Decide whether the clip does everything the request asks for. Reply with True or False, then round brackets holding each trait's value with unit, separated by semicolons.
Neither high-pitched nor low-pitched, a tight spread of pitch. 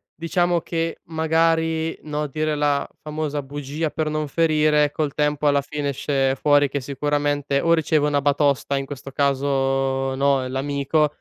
True (145 Hz; 1.8 semitones)